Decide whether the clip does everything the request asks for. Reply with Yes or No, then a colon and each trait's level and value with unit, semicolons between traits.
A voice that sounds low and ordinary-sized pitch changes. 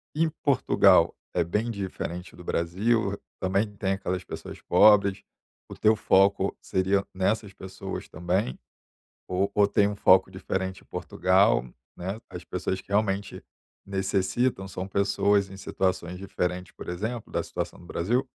No: very low, 95 Hz; narrow, 1.8 semitones